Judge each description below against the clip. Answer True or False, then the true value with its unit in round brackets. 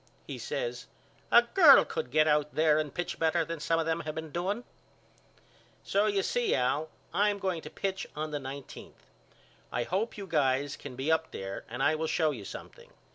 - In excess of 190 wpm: True (200 wpm)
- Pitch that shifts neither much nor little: True (4.6 semitones)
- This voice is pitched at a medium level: True (160 Hz)